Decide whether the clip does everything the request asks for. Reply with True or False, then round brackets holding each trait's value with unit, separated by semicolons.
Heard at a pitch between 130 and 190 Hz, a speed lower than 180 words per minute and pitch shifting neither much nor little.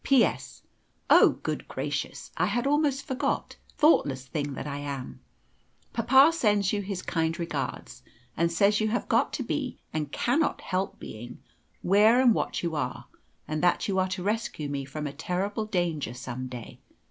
False (185 Hz; 170 wpm; 7.3 semitones)